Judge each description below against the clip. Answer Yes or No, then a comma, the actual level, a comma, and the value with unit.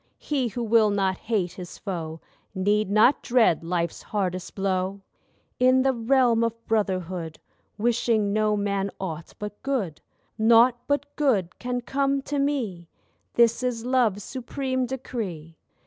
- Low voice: No, high, 215 Hz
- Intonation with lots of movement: No, average, 4.9 semitones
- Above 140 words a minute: No, slow, 135 wpm